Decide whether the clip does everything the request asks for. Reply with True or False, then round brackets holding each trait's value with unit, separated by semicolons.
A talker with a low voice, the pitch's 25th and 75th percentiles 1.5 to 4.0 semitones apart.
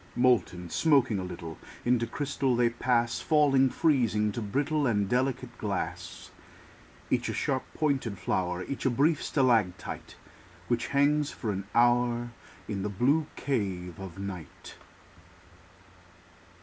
False (120 Hz; 5.2 semitones)